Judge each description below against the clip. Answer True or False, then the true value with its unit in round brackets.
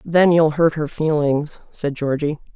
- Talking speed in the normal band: True (165 wpm)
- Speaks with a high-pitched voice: False (155 Hz)